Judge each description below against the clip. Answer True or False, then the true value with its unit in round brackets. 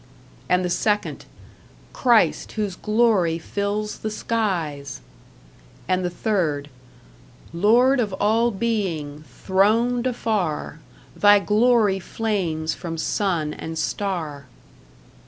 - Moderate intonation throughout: True (5.0 semitones)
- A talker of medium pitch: False (200 Hz)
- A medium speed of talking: False (100 wpm)